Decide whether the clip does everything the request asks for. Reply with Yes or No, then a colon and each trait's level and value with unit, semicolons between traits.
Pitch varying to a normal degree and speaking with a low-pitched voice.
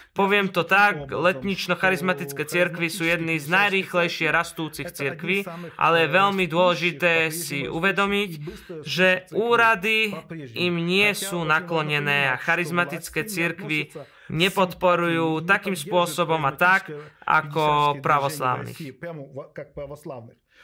No: average, 3.0 semitones; medium, 170 Hz